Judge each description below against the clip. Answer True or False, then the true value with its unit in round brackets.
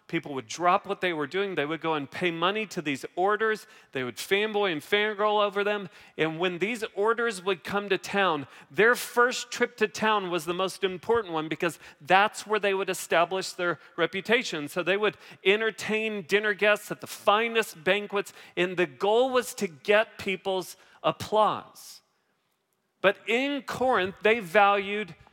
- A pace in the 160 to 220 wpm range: True (170 wpm)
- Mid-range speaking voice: False (200 Hz)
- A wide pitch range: False (3.2 semitones)